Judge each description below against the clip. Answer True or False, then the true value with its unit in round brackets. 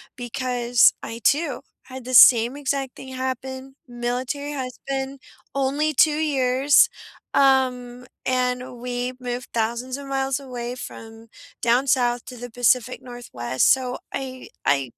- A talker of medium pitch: False (255 Hz)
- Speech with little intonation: True (1.7 semitones)